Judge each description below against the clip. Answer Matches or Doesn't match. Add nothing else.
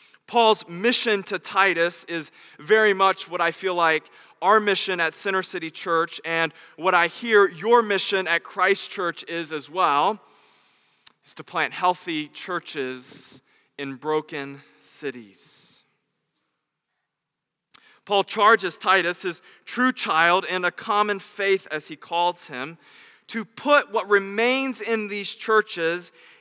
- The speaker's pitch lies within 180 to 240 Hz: Matches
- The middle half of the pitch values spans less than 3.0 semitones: Doesn't match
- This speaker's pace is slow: Matches